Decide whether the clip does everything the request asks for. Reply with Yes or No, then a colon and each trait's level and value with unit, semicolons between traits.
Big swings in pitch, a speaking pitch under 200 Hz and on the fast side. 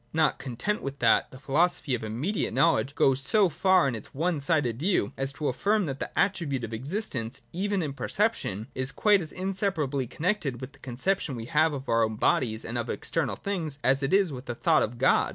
Yes: wide, 6.4 semitones; medium, 140 Hz; fast, 215 wpm